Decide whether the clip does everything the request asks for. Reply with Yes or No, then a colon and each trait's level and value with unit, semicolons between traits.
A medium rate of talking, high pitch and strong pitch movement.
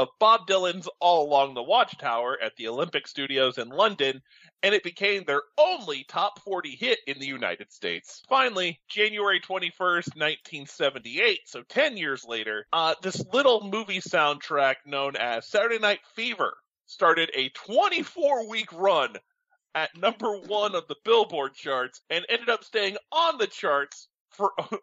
Yes: average, 150 wpm; high, 195 Hz; wide, 8.2 semitones